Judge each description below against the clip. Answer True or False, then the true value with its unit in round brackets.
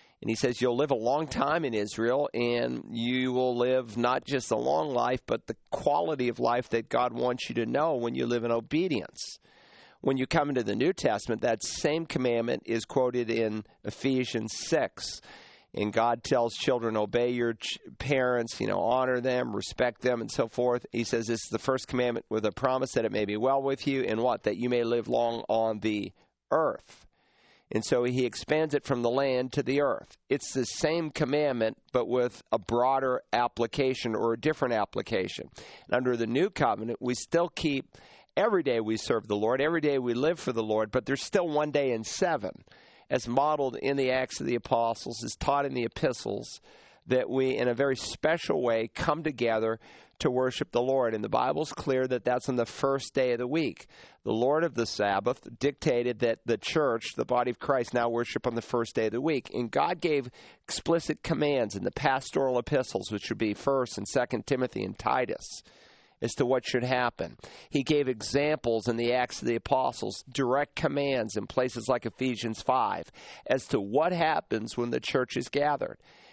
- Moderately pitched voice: False (125 Hz)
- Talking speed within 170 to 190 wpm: False (200 wpm)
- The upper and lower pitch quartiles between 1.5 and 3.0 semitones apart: True (2.6 semitones)